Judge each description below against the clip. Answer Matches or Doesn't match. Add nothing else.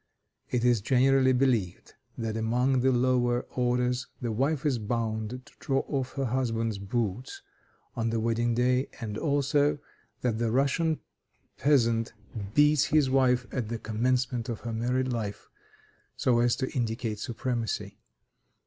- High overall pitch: Doesn't match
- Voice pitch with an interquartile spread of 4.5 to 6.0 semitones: Doesn't match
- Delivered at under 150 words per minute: Matches